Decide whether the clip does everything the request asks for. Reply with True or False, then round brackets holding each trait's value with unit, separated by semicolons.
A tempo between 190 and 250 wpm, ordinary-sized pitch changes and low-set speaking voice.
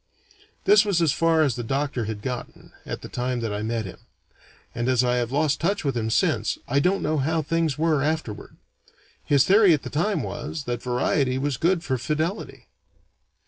False (195 wpm; 4.9 semitones; 145 Hz)